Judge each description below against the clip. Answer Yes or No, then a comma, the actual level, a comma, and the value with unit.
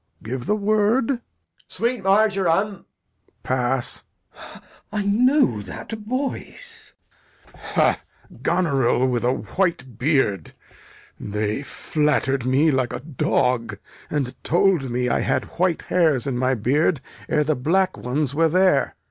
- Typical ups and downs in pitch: No, wide, 7.5 semitones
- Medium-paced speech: No, slow, 130 wpm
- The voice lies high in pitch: No, medium, 150 Hz